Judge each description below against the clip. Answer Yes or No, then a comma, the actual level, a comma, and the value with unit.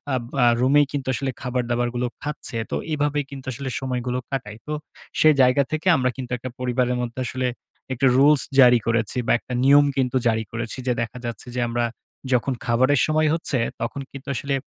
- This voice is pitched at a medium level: No, low, 130 Hz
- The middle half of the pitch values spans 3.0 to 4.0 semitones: No, narrow, 2.4 semitones